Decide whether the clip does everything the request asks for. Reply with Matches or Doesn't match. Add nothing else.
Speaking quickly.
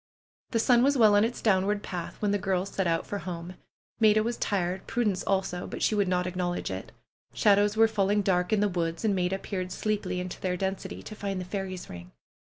Matches